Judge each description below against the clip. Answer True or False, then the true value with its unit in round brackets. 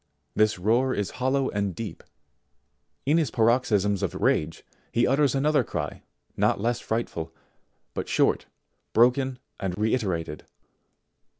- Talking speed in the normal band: False (120 wpm)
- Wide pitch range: False (4.4 semitones)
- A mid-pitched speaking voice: False (115 Hz)